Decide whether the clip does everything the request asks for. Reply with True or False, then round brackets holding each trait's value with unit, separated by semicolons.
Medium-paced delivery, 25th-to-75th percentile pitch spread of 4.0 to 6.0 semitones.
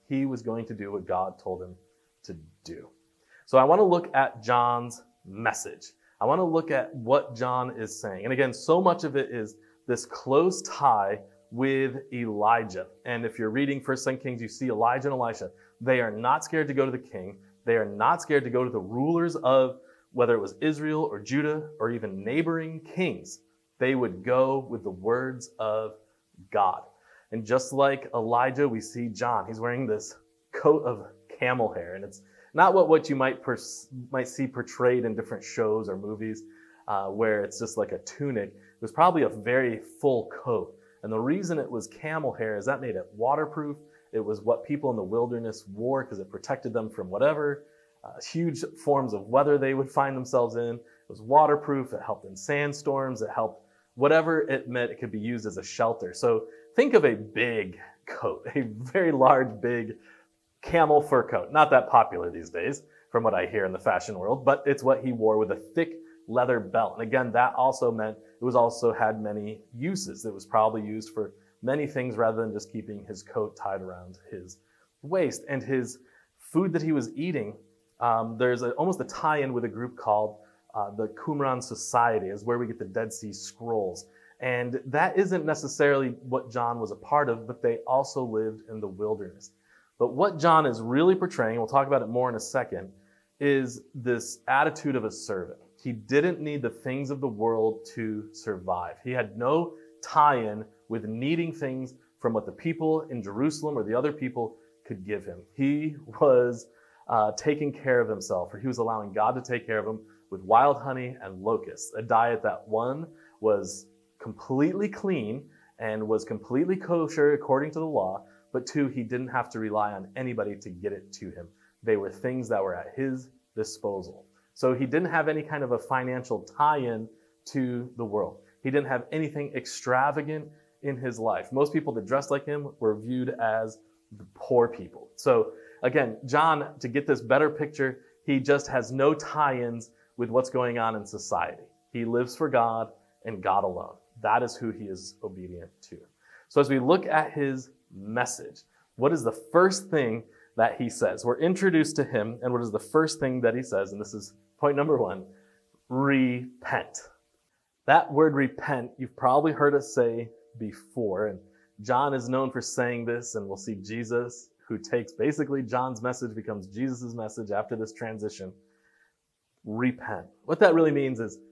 True (190 wpm; 4.6 semitones)